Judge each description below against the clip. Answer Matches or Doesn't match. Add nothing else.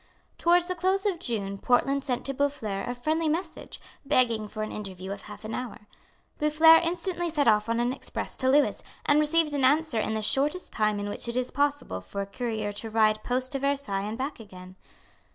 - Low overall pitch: Doesn't match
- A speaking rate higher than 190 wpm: Matches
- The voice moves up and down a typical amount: Doesn't match